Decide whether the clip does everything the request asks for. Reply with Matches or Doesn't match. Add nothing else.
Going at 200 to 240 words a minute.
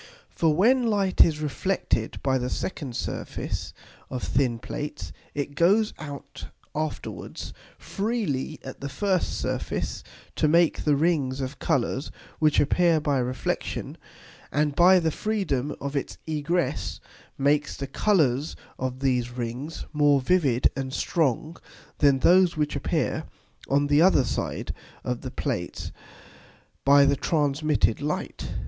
Doesn't match